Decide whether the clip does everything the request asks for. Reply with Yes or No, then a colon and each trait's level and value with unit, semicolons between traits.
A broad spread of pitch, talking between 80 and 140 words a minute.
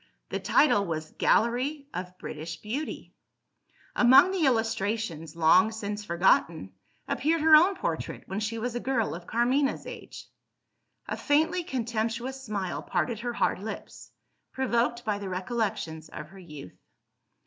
Yes: wide, 5.9 semitones; slow, 135 wpm